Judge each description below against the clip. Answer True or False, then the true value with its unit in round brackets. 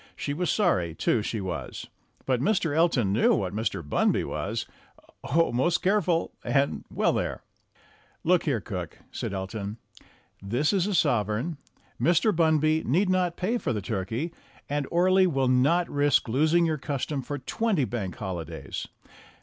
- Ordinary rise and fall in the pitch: False (7.9 semitones)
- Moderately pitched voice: True (145 Hz)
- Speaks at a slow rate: False (150 wpm)